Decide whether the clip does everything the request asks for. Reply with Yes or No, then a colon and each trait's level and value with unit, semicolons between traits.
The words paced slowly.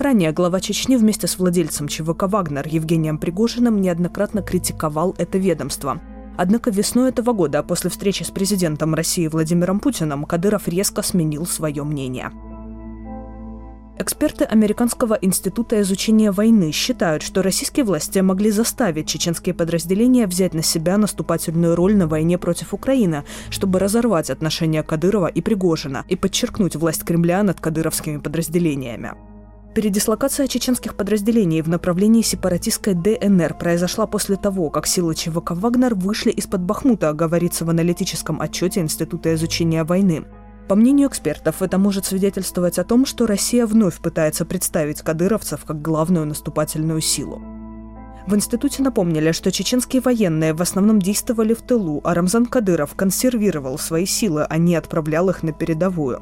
No: average, 140 wpm